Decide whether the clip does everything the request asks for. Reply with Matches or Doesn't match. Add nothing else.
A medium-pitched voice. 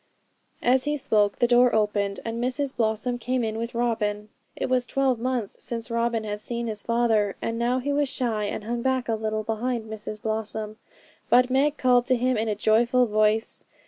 Doesn't match